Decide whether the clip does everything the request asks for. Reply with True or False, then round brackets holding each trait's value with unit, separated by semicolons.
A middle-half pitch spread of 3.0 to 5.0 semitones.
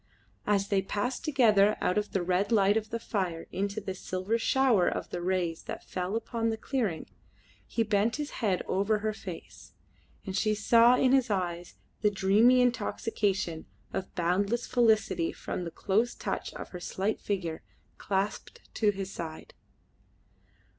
True (3.3 semitones)